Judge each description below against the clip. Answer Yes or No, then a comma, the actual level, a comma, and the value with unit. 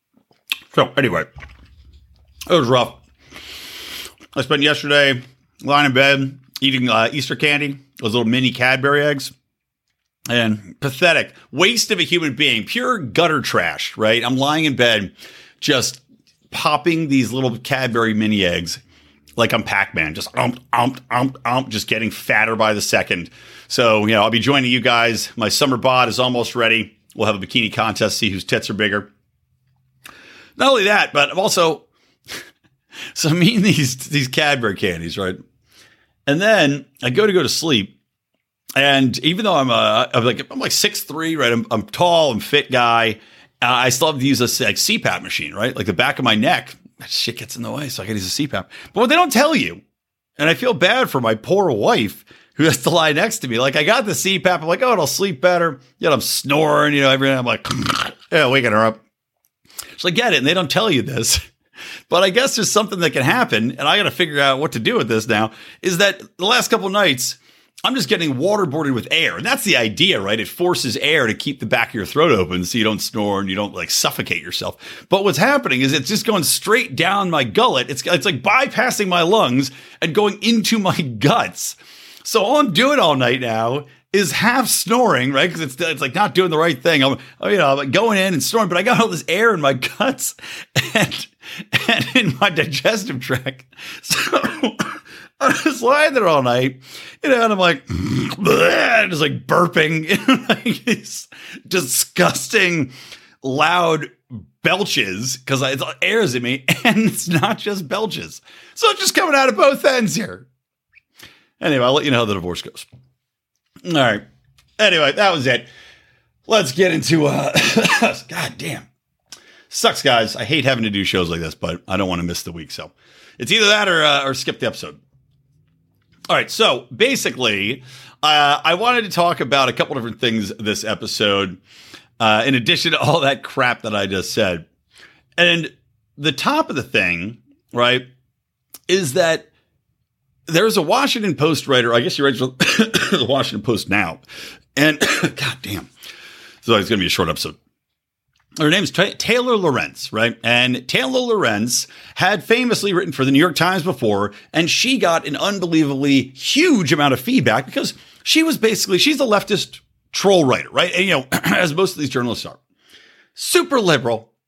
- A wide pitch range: Yes, wide, 7.1 semitones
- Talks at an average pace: Yes, average, 190 wpm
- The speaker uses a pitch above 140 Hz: No, low, 135 Hz